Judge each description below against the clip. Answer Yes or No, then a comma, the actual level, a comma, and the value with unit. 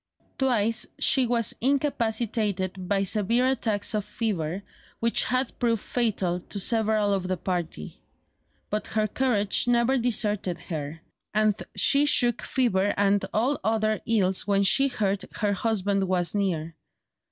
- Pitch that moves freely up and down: No, average, 3.5 semitones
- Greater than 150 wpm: No, average, 140 wpm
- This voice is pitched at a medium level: No, high, 210 Hz